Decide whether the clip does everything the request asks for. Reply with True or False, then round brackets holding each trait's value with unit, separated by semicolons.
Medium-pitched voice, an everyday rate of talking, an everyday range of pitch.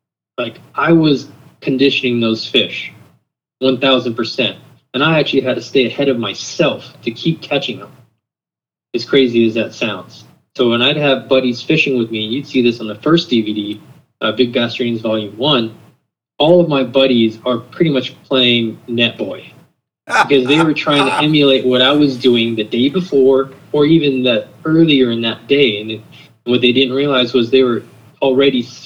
False (130 Hz; 180 wpm; 3.1 semitones)